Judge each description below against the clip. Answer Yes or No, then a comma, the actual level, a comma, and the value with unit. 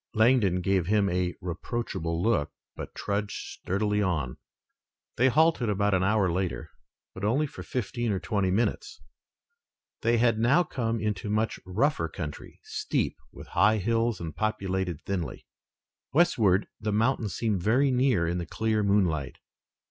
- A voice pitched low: Yes, low, 105 Hz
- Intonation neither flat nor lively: Yes, average, 4.0 semitones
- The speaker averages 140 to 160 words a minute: Yes, average, 145 wpm